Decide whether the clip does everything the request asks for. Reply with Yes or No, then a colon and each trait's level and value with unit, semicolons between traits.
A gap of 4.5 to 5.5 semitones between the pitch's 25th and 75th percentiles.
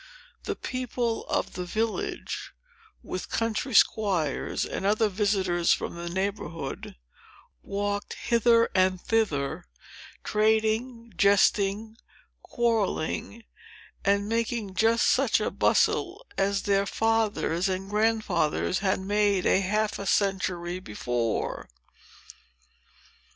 No: average, 3.1 semitones